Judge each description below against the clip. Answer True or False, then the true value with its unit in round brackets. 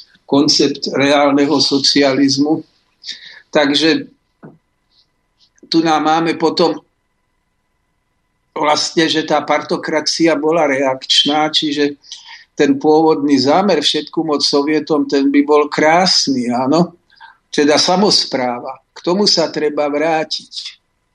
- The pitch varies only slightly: True (1.8 semitones)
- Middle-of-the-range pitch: True (150 Hz)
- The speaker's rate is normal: False (95 wpm)